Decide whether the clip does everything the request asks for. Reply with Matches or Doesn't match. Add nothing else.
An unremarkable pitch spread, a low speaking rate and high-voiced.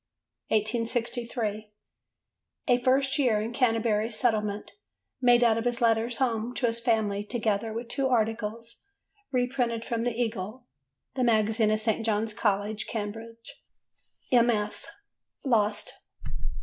Doesn't match